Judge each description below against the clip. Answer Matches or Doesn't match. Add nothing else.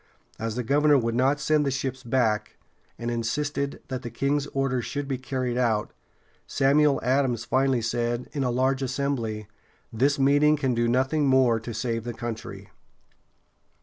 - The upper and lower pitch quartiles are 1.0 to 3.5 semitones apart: Matches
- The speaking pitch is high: Doesn't match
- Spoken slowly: Doesn't match